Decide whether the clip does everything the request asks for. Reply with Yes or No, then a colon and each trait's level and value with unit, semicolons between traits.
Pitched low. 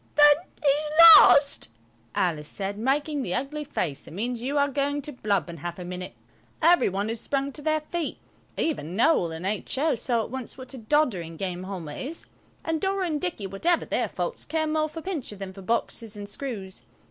No: very high, 255 Hz